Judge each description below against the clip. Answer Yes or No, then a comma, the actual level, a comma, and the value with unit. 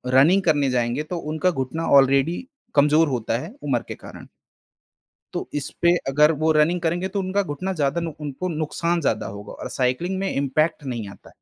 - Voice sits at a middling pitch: Yes, medium, 155 Hz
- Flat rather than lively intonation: No, average, 4.1 semitones